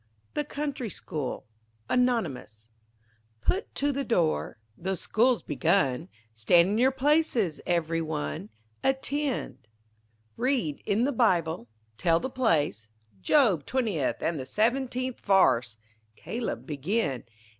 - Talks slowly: Yes, slow, 115 wpm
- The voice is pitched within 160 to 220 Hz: Yes, high, 190 Hz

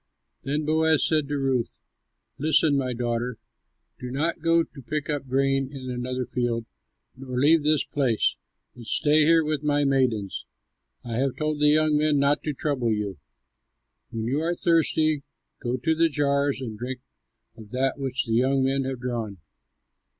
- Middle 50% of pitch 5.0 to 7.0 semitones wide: No, average, 3.4 semitones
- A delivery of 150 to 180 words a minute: Yes, average, 165 wpm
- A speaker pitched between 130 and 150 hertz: Yes, low, 135 Hz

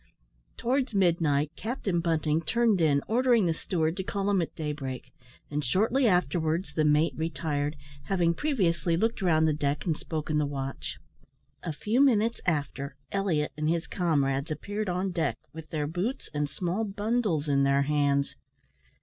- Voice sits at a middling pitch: Yes, medium, 165 Hz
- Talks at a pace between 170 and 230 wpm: No, average, 160 wpm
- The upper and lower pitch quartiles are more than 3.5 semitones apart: Yes, average, 4.8 semitones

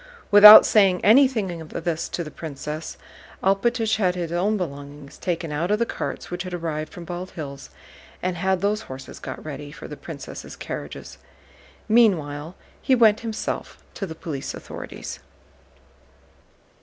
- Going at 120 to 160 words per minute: Yes, average, 150 wpm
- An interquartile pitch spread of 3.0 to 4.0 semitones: No, average, 5.1 semitones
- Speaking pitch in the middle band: Yes, medium, 175 Hz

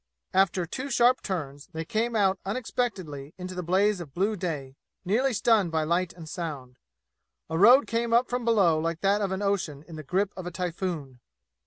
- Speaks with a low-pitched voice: No, medium, 185 Hz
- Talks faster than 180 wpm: Yes, average, 190 wpm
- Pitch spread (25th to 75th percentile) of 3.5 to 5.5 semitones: Yes, average, 4.6 semitones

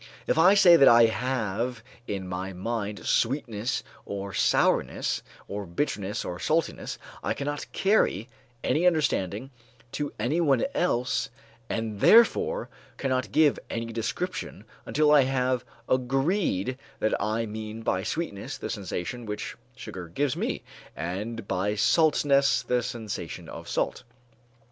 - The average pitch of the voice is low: Yes, low, 120 Hz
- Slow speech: Yes, slow, 125 wpm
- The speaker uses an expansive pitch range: Yes, wide, 5.7 semitones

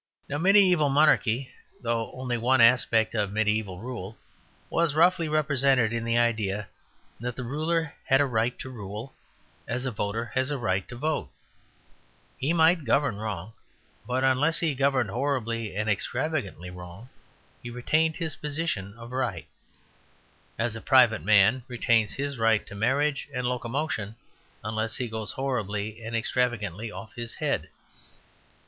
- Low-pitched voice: Yes, low, 120 Hz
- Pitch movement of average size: Yes, average, 4.2 semitones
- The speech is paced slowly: No, average, 145 wpm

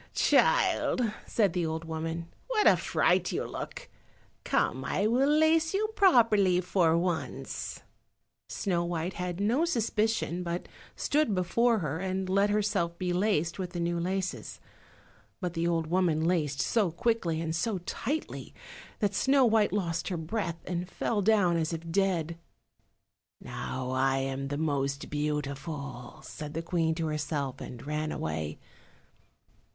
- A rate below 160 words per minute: Yes, average, 145 wpm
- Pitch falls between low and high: Yes, medium, 175 Hz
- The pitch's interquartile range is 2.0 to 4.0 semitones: No, average, 4.5 semitones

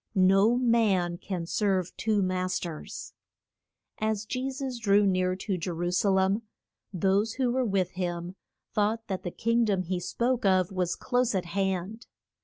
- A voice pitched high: Yes, high, 195 Hz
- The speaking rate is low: No, average, 165 wpm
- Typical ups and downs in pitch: Yes, average, 3.4 semitones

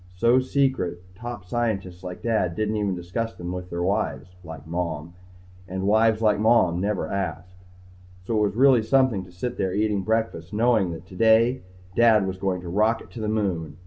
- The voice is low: Yes, low, 100 Hz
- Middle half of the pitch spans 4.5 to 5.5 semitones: No, average, 4.0 semitones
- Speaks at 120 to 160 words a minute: No, average, 175 wpm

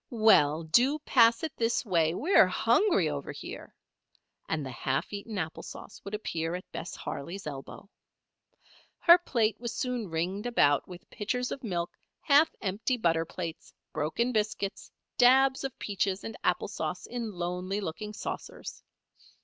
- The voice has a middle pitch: No, high, 205 Hz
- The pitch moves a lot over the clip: Yes, wide, 6.3 semitones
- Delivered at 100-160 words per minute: Yes, average, 150 wpm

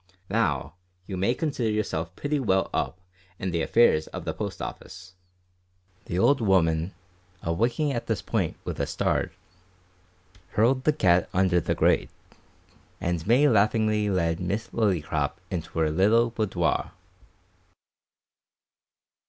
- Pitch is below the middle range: Yes, very low, 95 Hz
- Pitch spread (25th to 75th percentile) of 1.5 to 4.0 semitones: No, average, 5.2 semitones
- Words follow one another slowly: Yes, slow, 130 wpm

